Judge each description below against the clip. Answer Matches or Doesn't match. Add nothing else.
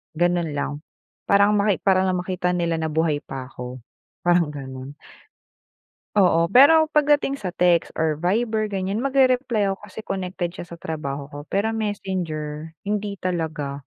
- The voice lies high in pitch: Doesn't match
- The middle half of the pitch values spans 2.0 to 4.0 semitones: Doesn't match